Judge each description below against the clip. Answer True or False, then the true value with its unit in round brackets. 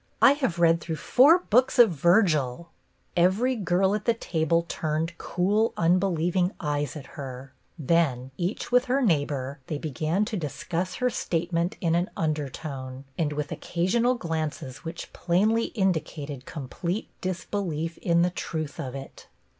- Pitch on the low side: False (170 Hz)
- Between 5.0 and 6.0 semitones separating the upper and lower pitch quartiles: False (4.2 semitones)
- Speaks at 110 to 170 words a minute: True (150 wpm)